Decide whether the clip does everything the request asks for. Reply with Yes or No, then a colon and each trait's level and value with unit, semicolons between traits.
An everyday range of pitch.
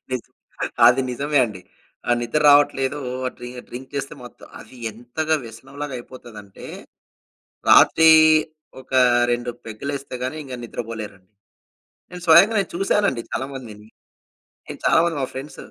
Yes: average, 3.5 semitones